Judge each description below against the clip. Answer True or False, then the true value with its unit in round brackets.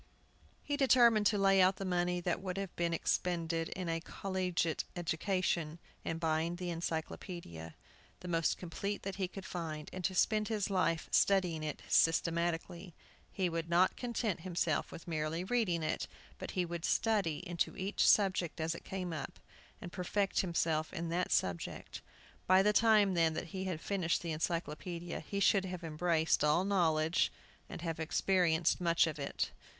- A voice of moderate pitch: True (175 Hz)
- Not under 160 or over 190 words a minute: True (165 wpm)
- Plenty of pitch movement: False (2.6 semitones)